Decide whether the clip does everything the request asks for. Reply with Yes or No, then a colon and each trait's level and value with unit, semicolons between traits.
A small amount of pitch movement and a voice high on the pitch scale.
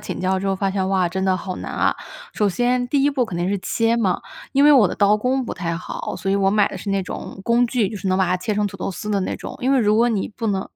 No: average, 3.7 semitones; high, 200 Hz